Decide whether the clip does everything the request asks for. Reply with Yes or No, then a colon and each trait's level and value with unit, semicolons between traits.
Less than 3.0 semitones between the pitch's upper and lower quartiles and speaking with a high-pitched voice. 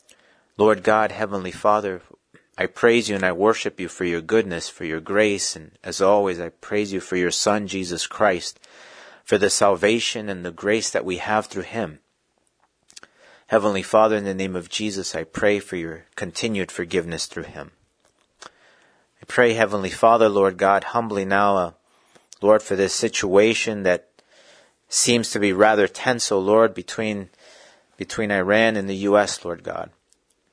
No: narrow, 2.6 semitones; low, 100 Hz